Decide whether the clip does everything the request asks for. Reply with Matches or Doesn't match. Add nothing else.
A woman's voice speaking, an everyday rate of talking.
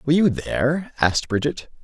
Doesn't match